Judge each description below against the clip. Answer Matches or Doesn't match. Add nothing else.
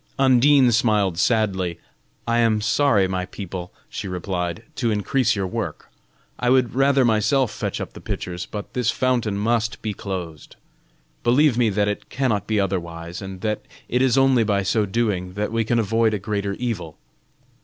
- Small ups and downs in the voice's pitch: Doesn't match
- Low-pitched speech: Matches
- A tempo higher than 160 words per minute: Matches